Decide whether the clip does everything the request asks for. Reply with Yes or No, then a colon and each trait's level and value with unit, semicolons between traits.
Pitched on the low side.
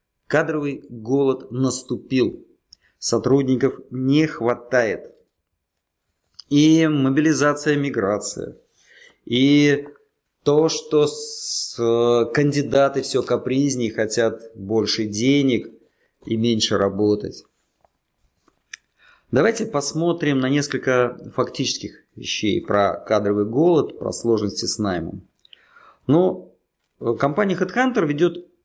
Yes: low, 130 Hz